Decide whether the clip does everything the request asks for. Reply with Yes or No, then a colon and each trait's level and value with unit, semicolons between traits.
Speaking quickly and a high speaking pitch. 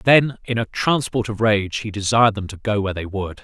No: fast, 245 wpm; low, 105 Hz